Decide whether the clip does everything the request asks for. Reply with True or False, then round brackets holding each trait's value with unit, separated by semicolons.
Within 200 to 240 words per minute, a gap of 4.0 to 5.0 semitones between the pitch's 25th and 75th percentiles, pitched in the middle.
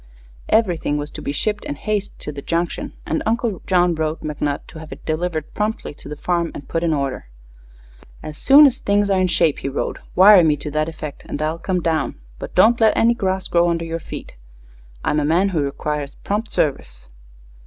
True (205 wpm; 4.4 semitones; 165 Hz)